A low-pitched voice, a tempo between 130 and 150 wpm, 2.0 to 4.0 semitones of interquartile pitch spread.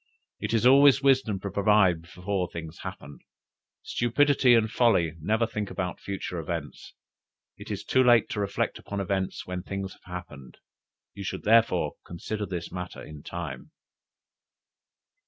No: very low, 95 Hz; average, 145 wpm; average, 4.4 semitones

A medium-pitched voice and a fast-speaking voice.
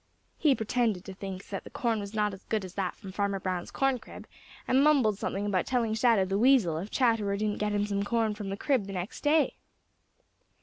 No: high, 210 Hz; fast, 220 wpm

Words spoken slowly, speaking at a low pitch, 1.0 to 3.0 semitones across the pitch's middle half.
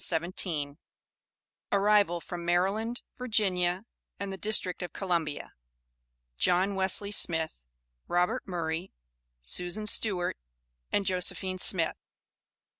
No: slow, 90 wpm; medium, 185 Hz; narrow, 2.5 semitones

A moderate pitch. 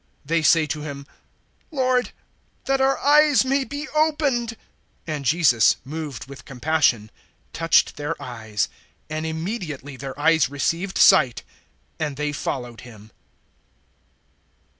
Yes: medium, 155 Hz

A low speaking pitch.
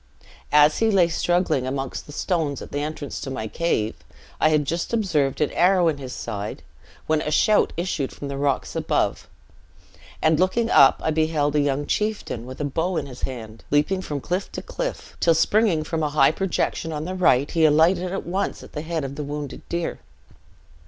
No: medium, 155 Hz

